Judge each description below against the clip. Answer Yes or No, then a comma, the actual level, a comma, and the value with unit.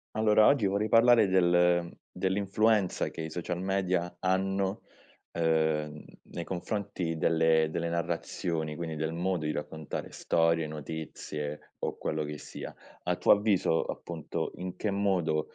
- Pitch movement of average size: Yes, average, 3.3 semitones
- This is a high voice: No, very low, 85 Hz